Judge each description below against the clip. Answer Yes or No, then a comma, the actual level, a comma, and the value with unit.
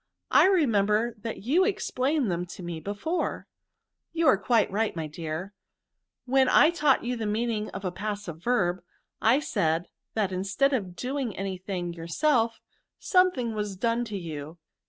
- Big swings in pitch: Yes, wide, 5.7 semitones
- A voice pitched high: Yes, high, 210 Hz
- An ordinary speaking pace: Yes, average, 165 wpm